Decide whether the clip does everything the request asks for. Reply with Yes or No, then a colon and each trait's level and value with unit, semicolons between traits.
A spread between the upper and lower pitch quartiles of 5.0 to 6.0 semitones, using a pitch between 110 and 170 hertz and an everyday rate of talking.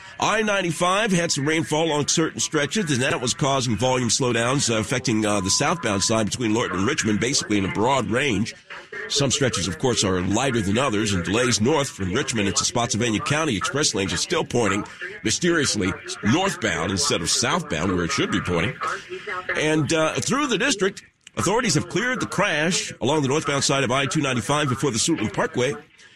Yes: wide, 5.6 semitones; medium, 140 Hz; average, 180 wpm